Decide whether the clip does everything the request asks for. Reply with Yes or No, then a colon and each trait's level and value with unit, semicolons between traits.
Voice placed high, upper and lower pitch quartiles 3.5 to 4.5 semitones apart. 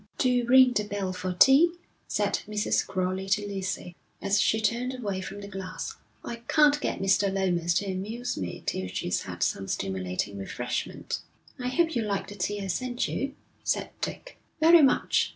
No: high, 200 Hz; average, 5.1 semitones